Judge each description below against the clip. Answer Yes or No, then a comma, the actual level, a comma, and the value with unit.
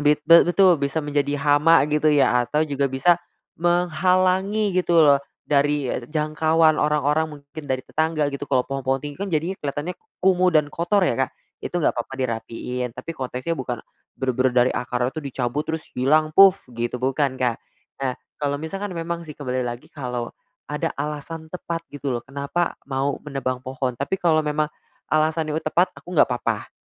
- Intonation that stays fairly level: No, average, 3.7 semitones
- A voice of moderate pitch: Yes, medium, 150 Hz